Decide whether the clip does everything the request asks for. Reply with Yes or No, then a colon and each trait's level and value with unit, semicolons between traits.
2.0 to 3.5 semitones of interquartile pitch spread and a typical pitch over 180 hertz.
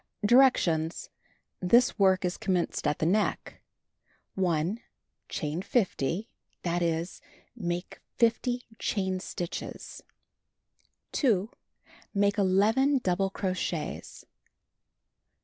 No: average, 4.1 semitones; high, 190 Hz